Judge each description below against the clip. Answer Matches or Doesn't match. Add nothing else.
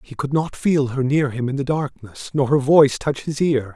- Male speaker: Matches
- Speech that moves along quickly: Matches